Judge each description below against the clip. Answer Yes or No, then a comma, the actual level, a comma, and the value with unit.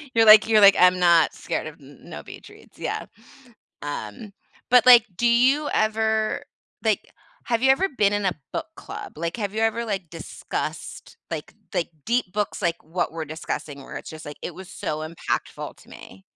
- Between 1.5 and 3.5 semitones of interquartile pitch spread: No, average, 5.3 semitones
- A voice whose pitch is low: No, high, 200 Hz